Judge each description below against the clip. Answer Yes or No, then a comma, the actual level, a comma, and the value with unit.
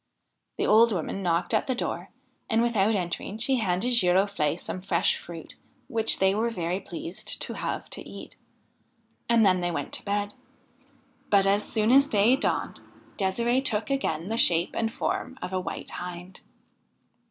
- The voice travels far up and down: No, average, 4.1 semitones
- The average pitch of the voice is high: Yes, high, 200 Hz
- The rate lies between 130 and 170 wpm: Yes, average, 165 wpm